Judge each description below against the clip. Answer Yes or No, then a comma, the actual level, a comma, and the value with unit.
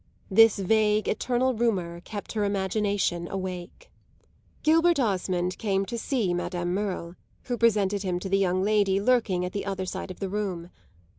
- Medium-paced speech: Yes, average, 160 wpm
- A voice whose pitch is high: Yes, high, 195 Hz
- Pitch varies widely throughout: No, average, 3.0 semitones